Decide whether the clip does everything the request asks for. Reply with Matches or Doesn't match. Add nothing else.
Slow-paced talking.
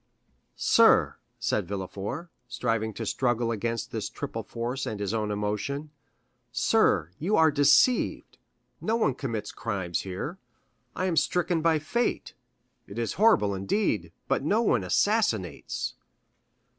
Matches